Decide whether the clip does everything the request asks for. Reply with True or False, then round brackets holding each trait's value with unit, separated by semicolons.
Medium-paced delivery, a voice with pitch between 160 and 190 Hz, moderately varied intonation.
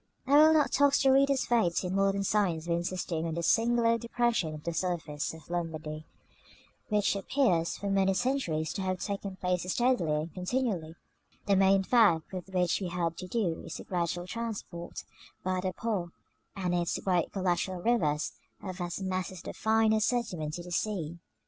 True (180 wpm; 185 Hz; 4.3 semitones)